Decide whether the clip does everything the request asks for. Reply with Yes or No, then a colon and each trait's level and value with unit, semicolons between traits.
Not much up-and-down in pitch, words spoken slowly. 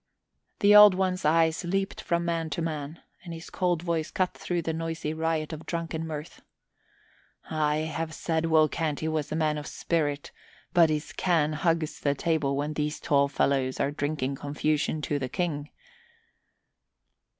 No: narrow, 1.9 semitones; average, 160 wpm